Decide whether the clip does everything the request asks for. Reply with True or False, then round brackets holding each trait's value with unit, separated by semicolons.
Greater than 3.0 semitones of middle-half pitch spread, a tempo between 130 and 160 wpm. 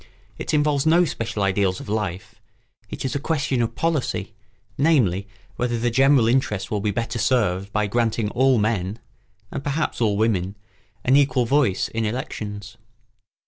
True (4.6 semitones; 155 wpm)